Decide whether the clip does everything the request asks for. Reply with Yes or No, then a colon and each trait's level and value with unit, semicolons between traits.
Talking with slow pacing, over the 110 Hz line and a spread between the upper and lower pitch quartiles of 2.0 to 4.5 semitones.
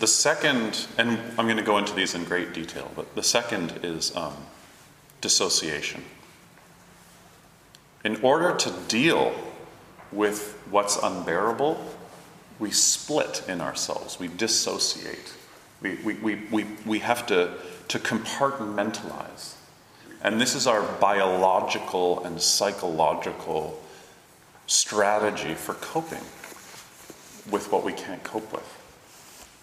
No: slow, 115 wpm; low, 105 Hz; average, 2.8 semitones